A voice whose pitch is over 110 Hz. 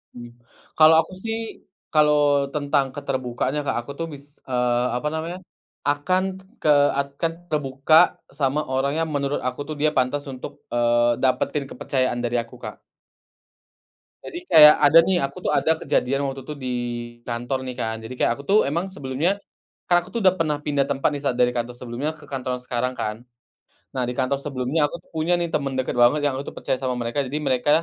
Yes: medium, 140 Hz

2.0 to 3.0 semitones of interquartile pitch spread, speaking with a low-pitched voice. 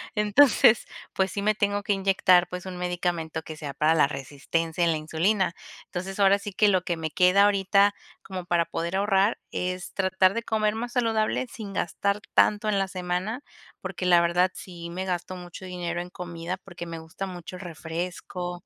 No: narrow, 2.6 semitones; medium, 185 Hz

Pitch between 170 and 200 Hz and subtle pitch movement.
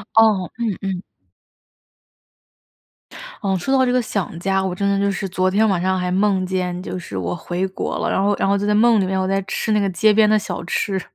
Yes: high, 195 Hz; narrow, 2.1 semitones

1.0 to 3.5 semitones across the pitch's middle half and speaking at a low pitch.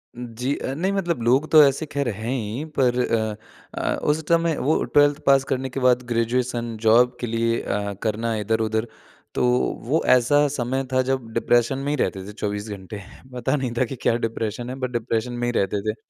Yes: average, 3.1 semitones; low, 120 Hz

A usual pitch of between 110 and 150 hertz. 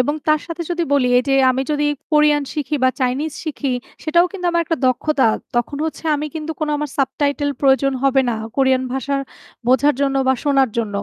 No: very high, 285 Hz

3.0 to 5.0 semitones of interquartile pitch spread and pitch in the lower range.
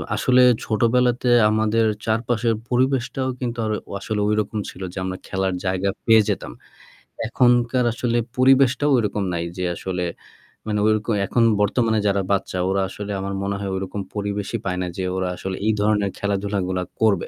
Yes: average, 3.4 semitones; low, 105 Hz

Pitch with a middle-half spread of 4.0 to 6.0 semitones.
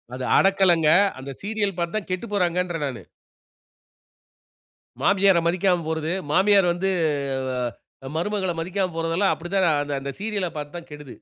No: average, 3.3 semitones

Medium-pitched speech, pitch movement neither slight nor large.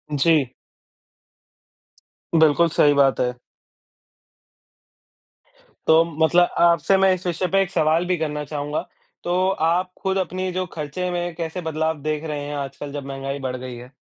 Yes: medium, 160 Hz; average, 3.5 semitones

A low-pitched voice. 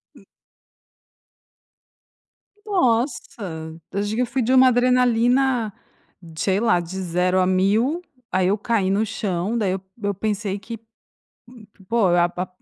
No: high, 215 Hz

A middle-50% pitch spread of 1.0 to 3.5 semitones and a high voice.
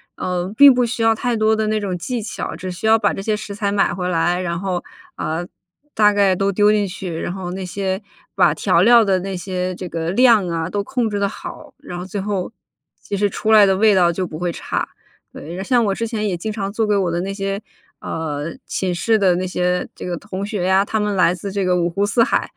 Yes: average, 2.9 semitones; high, 195 Hz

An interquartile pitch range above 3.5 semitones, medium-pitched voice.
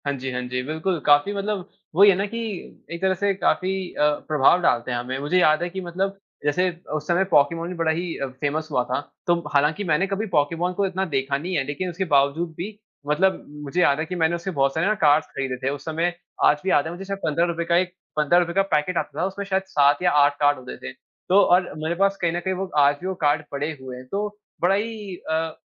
Yes: average, 4.4 semitones; medium, 170 Hz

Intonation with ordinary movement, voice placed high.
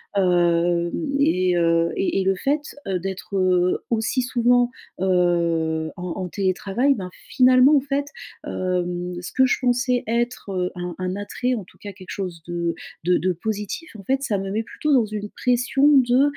No: wide, 5.7 semitones; high, 195 Hz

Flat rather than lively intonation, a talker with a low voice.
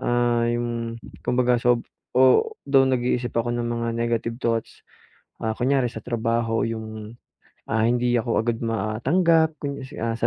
Yes: narrow, 1.4 semitones; low, 120 Hz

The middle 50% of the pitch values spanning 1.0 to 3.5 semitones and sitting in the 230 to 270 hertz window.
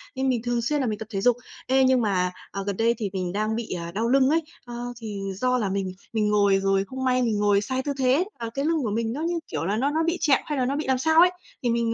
No: average, 4.3 semitones; high, 235 Hz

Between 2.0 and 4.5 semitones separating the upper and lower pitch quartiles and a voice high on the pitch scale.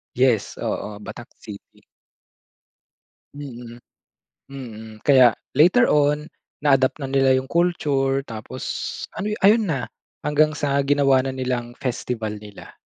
No: average, 3.1 semitones; low, 135 Hz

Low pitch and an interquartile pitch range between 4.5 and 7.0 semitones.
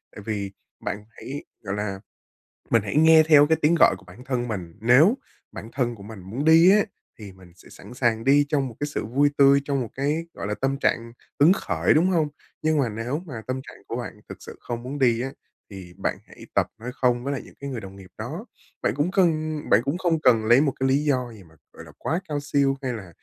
Yes: low, 130 Hz; average, 4.9 semitones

